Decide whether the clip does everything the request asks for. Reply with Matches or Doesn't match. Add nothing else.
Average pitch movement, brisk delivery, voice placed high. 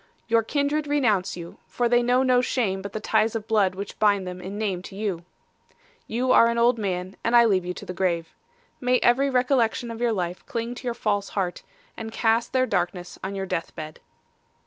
Matches